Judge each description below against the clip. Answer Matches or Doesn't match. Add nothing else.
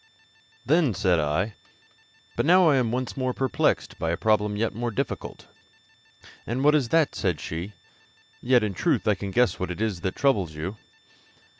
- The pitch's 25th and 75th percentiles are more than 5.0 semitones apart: Matches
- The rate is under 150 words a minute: Doesn't match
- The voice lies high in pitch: Doesn't match